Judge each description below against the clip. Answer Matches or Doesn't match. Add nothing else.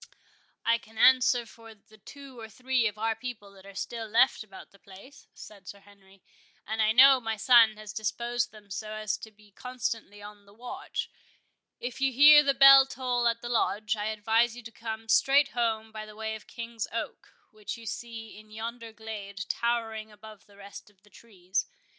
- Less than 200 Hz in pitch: Doesn't match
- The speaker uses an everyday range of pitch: Doesn't match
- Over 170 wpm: Matches